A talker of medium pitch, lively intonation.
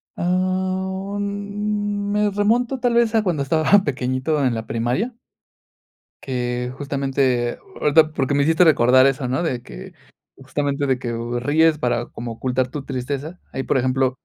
Yes: medium, 145 Hz; wide, 6.8 semitones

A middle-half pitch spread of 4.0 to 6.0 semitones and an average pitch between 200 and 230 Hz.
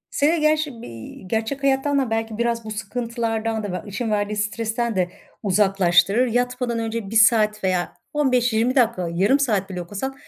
No: average, 3.3 semitones; high, 225 Hz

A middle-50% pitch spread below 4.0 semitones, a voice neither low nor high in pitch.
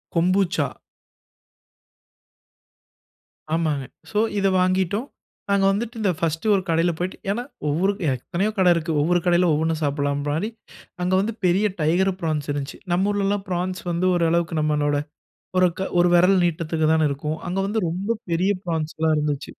Yes: average, 3.5 semitones; medium, 175 Hz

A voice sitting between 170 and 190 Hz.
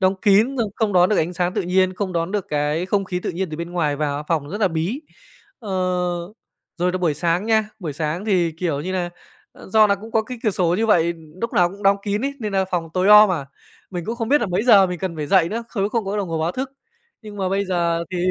Yes: medium, 185 Hz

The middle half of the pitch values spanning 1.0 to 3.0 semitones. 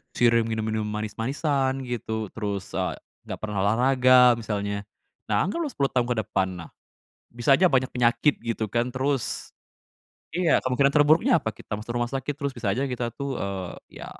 No: average, 3.7 semitones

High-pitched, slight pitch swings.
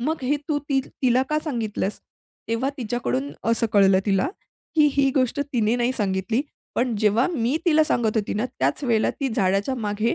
No: high, 235 Hz; average, 4.3 semitones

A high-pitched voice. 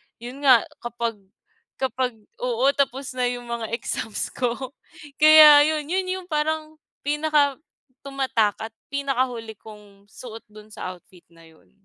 Yes: very high, 255 Hz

